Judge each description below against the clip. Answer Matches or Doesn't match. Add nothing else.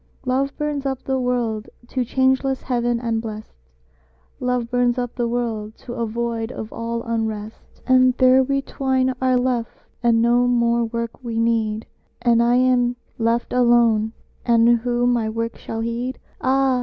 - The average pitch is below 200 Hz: Doesn't match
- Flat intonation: Matches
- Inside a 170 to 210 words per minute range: Doesn't match